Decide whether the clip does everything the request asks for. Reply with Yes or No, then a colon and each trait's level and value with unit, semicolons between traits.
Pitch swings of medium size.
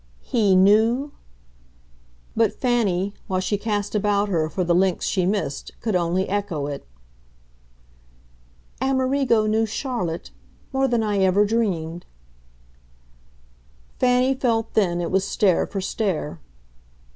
Yes: average, 4.2 semitones